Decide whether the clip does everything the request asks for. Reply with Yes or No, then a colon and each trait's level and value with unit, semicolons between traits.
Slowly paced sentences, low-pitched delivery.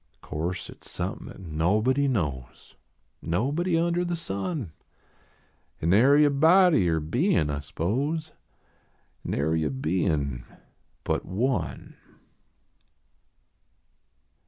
Yes: slow, 105 wpm; low, 100 Hz